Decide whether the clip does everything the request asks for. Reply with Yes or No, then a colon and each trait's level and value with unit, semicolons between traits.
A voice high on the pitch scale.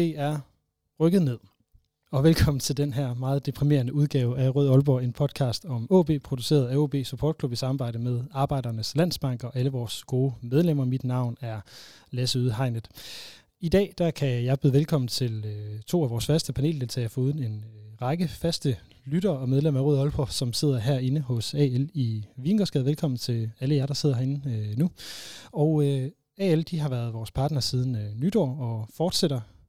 No: low, 135 Hz